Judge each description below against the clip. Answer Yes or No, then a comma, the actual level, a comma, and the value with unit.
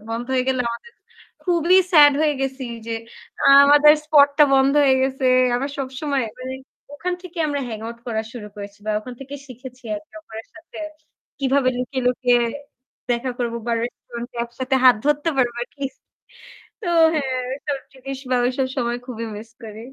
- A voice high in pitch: Yes, very high, 260 Hz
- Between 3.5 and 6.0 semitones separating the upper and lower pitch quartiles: No, average, 2.9 semitones